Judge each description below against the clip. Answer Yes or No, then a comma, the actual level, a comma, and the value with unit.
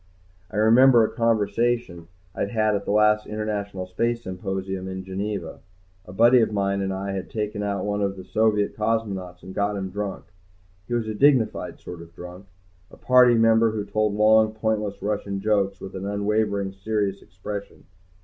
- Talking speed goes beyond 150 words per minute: Yes, average, 175 wpm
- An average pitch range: No, narrow, 2.2 semitones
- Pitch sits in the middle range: No, low, 105 Hz